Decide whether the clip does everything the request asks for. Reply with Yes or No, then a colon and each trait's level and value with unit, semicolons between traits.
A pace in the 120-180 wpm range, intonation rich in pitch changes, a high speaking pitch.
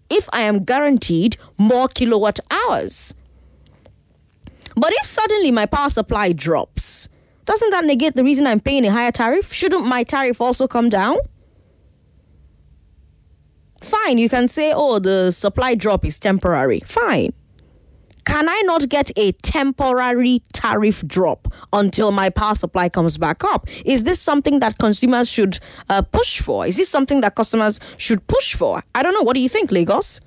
Yes: average, 160 wpm; wide, 6.5 semitones; high, 235 Hz